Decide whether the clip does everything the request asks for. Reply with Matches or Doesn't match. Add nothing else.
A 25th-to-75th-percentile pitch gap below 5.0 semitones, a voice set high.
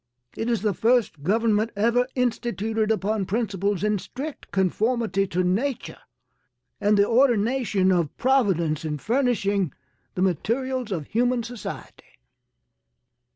Matches